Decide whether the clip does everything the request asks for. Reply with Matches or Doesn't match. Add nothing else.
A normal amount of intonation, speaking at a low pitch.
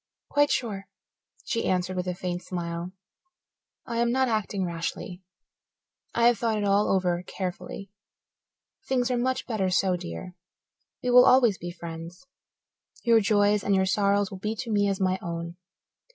Doesn't match